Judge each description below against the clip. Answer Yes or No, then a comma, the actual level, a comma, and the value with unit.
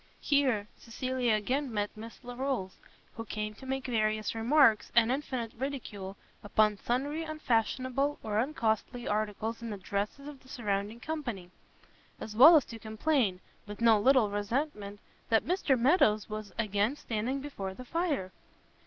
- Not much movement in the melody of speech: No, average, 4.1 semitones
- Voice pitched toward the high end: Yes, high, 230 Hz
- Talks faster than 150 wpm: No, average, 145 wpm